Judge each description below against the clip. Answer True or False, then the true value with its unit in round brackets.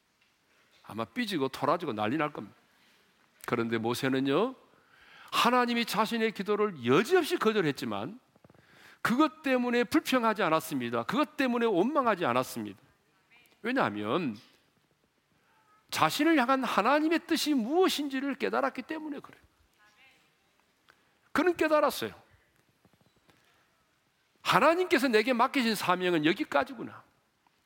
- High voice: True (245 Hz)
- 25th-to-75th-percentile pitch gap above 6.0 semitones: True (7.5 semitones)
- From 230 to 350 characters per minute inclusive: True (270 characters per minute)